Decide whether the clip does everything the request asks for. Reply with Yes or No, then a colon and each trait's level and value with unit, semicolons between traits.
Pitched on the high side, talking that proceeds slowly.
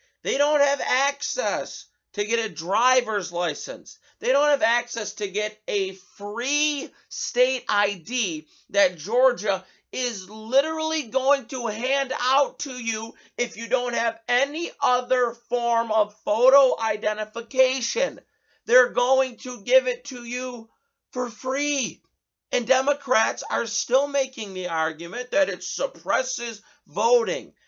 Yes: very high, 250 Hz; slow, 130 wpm